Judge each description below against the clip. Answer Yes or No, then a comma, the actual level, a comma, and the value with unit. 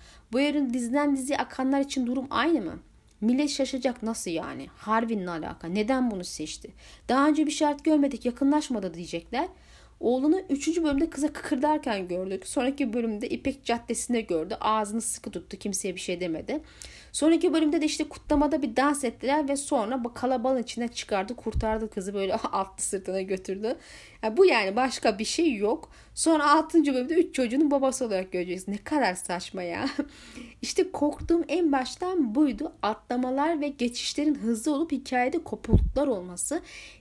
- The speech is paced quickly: Yes, fast, 155 wpm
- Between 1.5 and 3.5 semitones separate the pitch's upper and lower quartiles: No, average, 5.3 semitones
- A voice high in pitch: Yes, very high, 260 Hz